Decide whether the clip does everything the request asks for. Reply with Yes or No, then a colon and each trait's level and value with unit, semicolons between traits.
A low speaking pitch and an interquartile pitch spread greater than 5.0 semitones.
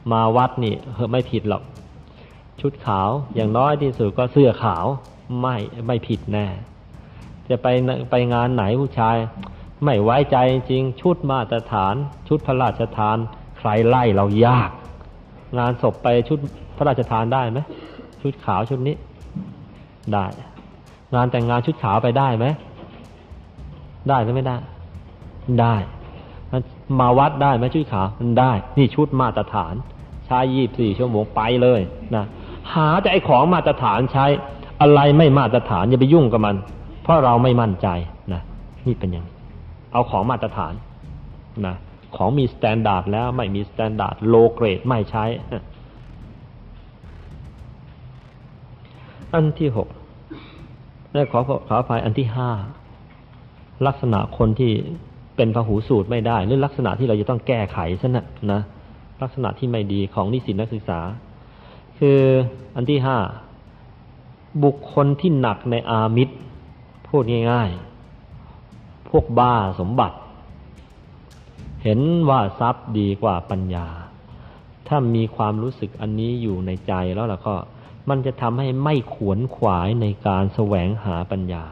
No: low, 120 Hz; average, 4.1 semitones